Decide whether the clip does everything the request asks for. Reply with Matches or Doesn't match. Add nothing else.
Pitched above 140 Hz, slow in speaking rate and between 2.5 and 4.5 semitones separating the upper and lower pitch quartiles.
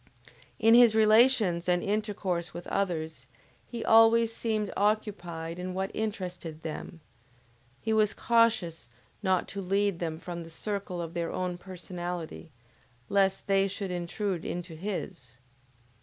Matches